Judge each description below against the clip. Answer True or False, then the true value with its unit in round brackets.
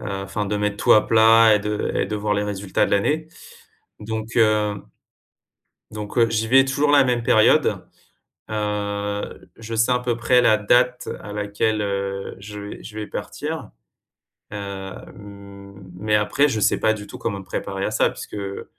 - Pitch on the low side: True (105 Hz)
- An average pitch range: False (1.8 semitones)